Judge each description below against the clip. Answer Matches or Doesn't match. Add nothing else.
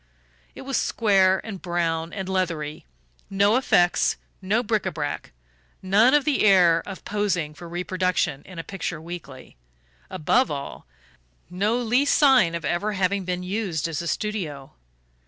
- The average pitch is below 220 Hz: Matches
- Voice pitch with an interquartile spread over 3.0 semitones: Matches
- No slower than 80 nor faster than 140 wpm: Doesn't match